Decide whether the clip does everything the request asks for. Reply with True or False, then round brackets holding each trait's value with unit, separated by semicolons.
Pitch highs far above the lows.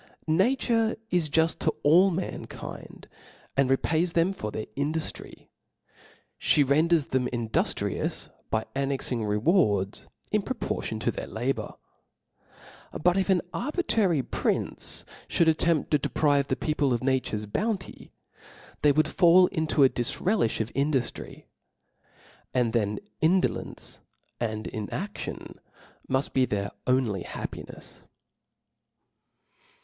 True (6.1 semitones)